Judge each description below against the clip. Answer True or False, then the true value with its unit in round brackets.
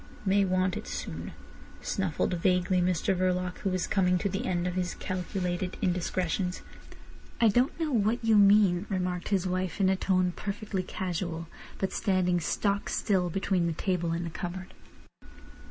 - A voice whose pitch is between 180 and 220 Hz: True (185 Hz)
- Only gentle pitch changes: True (1.7 semitones)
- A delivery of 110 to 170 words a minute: True (160 wpm)